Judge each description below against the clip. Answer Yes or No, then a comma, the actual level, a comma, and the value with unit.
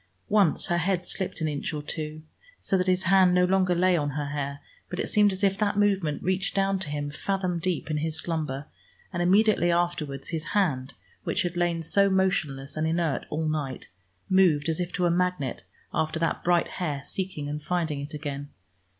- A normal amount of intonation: Yes, average, 3.7 semitones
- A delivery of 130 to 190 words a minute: No, average, 200 wpm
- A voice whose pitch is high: No, medium, 170 Hz